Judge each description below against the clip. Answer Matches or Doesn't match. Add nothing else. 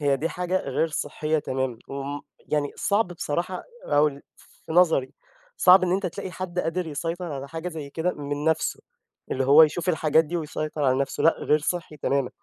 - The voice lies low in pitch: Doesn't match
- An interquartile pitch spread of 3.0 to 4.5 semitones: Matches